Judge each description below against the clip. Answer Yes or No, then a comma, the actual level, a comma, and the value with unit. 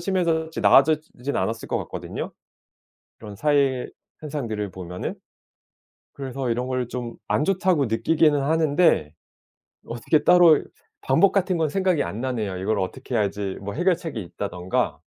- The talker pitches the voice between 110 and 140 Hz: Yes, low, 135 Hz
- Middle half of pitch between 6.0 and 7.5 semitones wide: Yes, wide, 6.6 semitones